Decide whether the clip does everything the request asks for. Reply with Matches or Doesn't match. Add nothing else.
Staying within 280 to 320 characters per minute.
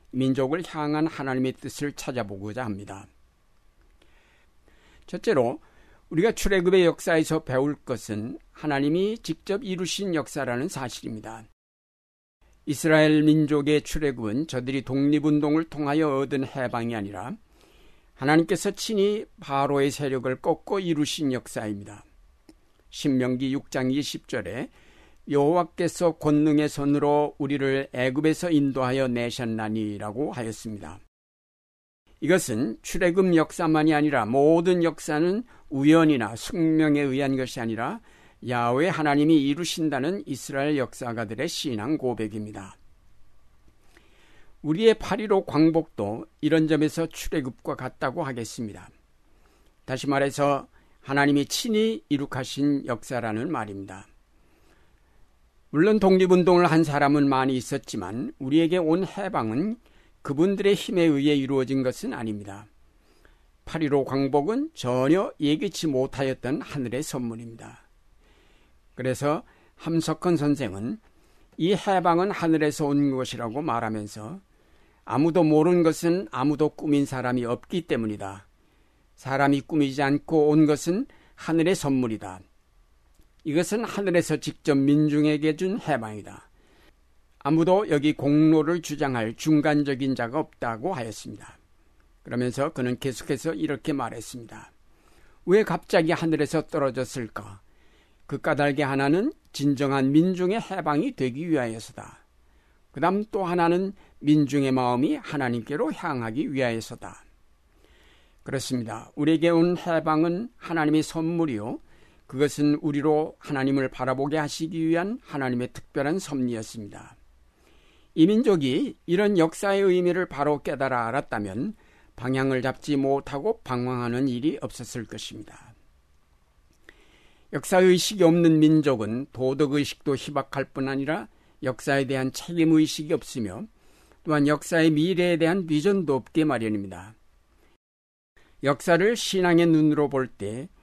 Matches